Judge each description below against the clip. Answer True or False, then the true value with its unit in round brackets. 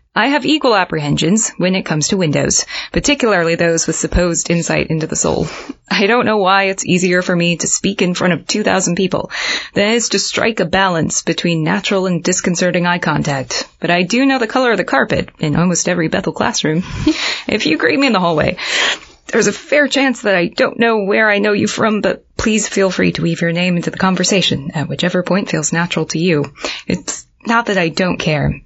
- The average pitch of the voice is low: False (185 Hz)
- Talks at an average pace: False (215 wpm)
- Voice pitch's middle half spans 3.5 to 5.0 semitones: True (3.8 semitones)